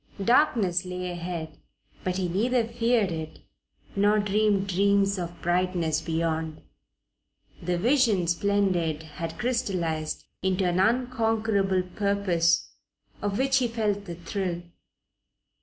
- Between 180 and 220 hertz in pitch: Yes, high, 190 Hz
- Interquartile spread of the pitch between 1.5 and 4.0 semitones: Yes, average, 3.5 semitones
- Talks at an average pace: No, slow, 110 wpm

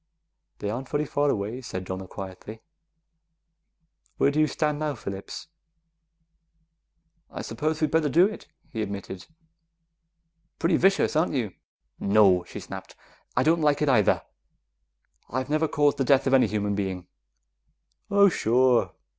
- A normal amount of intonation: No, wide, 6.9 semitones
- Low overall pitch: Yes, low, 130 Hz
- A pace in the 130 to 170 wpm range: Yes, average, 140 wpm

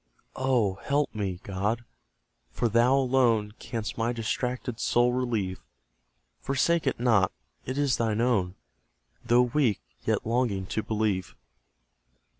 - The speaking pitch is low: Yes, low, 115 Hz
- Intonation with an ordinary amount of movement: Yes, average, 3.2 semitones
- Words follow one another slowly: Yes, slow, 120 wpm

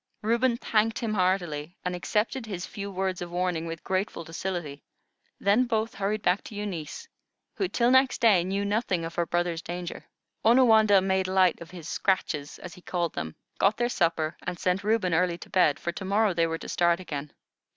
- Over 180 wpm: Yes, average, 195 wpm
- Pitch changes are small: No, average, 3.5 semitones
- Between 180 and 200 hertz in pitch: Yes, medium, 185 Hz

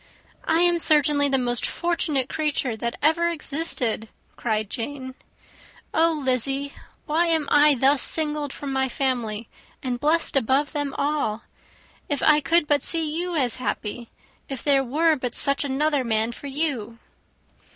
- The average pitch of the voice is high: Yes, very high, 280 Hz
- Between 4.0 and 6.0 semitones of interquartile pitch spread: No, average, 3.4 semitones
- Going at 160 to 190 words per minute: No, average, 150 wpm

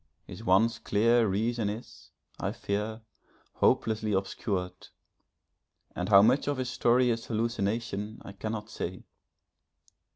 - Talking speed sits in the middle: No, slow, 120 wpm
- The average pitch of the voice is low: Yes, low, 110 Hz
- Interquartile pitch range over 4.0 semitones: No, average, 2.7 semitones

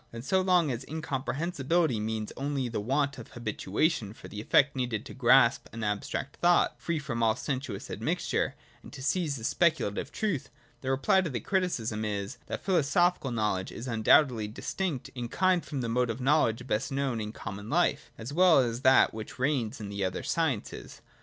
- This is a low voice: Yes, low, 130 Hz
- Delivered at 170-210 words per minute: Yes, average, 185 wpm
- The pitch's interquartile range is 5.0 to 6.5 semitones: Yes, wide, 5.5 semitones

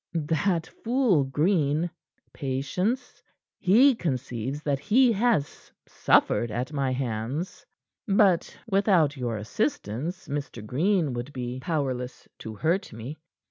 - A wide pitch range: Yes, wide, 6.8 semitones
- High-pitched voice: No, medium, 150 Hz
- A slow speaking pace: Yes, slow, 110 wpm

